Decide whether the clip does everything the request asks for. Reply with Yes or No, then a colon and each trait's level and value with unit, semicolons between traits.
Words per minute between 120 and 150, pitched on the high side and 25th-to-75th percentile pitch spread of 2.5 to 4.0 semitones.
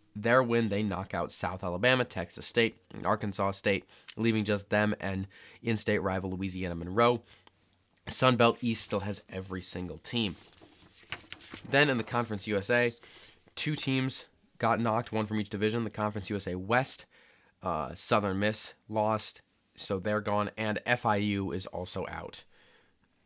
No: average, 145 wpm; low, 105 Hz; average, 3.2 semitones